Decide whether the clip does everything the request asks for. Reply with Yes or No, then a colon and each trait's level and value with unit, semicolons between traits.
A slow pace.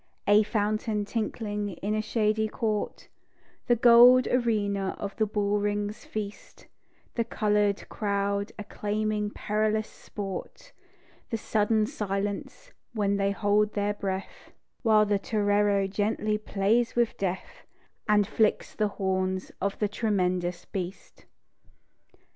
Yes: slow, 120 wpm